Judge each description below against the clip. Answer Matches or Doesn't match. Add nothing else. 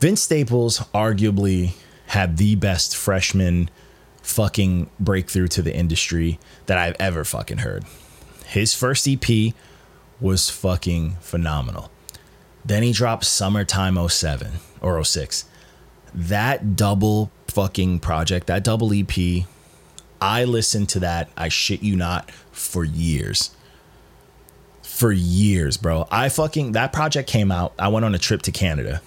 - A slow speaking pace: Matches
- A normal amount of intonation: Matches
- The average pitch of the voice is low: Matches